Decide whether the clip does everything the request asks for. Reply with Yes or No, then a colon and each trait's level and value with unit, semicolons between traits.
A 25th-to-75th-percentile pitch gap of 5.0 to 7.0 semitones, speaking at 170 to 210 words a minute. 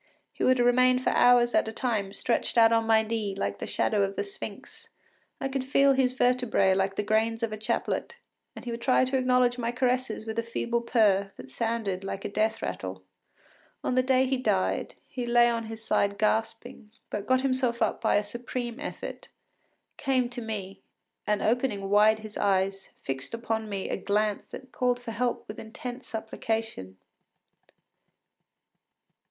No: average, 3.1 semitones; average, 180 wpm